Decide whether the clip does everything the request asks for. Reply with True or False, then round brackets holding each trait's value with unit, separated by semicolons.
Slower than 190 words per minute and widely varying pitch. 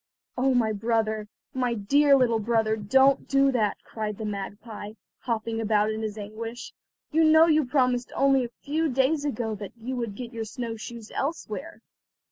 False (170 wpm; 3.7 semitones)